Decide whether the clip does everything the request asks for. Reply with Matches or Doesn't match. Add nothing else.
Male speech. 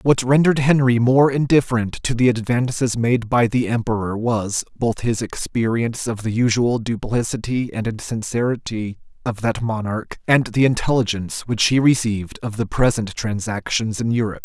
Matches